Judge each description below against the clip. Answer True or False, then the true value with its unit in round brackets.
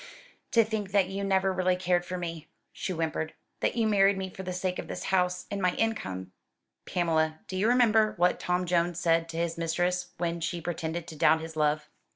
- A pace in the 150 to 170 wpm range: False (205 wpm)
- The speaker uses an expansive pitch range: False (2.6 semitones)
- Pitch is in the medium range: True (180 Hz)